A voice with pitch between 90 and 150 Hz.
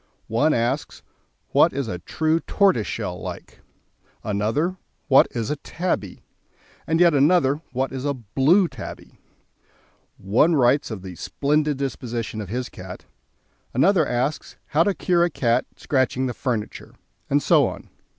Yes: low, 135 Hz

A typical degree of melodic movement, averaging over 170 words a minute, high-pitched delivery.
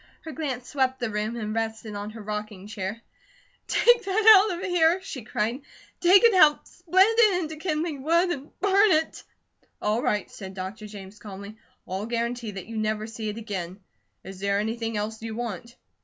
No: wide, 7.4 semitones; average, 185 wpm; high, 230 Hz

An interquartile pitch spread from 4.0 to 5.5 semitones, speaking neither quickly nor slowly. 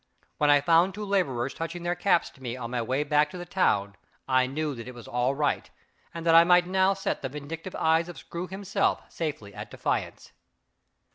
No: average, 5.2 semitones; fast, 210 wpm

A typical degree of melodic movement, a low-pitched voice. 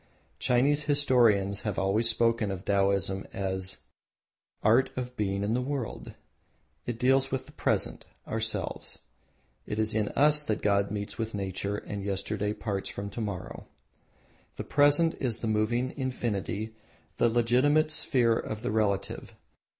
Yes: average, 3.9 semitones; low, 110 Hz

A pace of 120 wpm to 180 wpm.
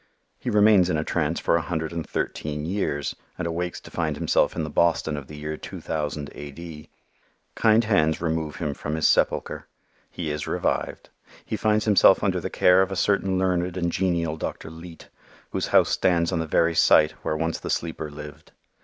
No: average, 195 wpm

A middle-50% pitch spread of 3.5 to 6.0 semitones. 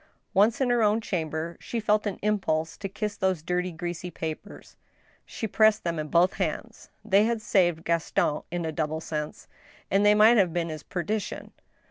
Yes: average, 4.5 semitones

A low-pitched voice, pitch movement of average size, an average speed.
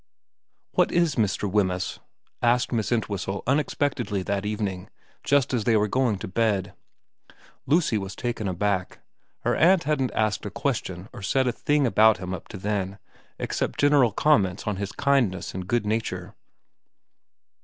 Yes: low, 105 Hz; average, 4.7 semitones; average, 160 wpm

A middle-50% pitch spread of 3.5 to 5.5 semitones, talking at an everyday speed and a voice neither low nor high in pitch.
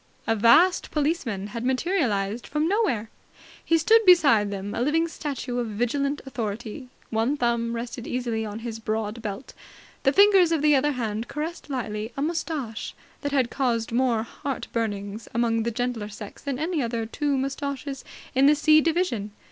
No: average, 4.8 semitones; average, 165 wpm; high, 245 Hz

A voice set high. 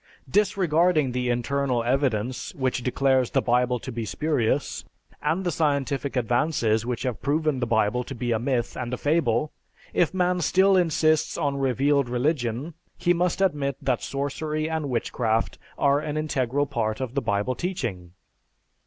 No: low, 135 Hz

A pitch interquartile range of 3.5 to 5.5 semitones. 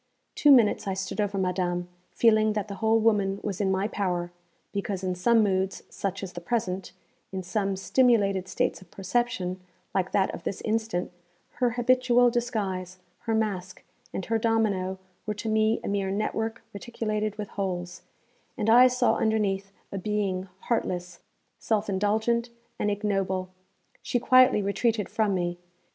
No: average, 2.9 semitones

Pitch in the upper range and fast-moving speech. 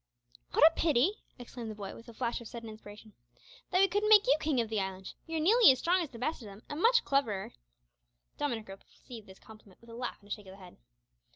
Yes: high, 235 Hz; fast, 245 wpm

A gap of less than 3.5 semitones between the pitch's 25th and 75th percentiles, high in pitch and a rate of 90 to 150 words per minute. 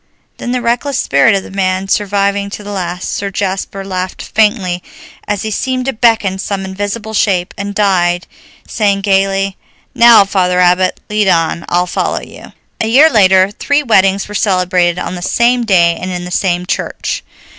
No: narrow, 2.4 semitones; high, 195 Hz; average, 175 wpm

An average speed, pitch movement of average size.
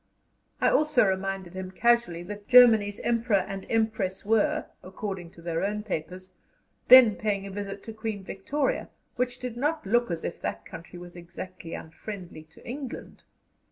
Yes: average, 160 wpm; average, 3.8 semitones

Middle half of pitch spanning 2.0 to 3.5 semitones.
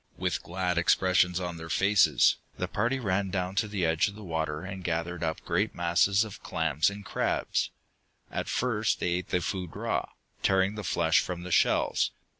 Yes: average, 2.8 semitones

